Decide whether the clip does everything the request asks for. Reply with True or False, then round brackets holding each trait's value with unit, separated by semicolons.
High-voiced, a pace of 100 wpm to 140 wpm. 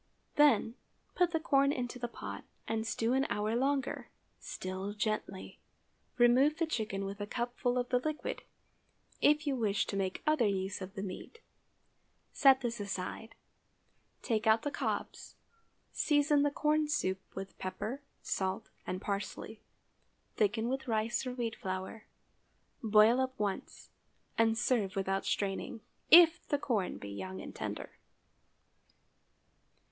True (225 Hz; 135 wpm)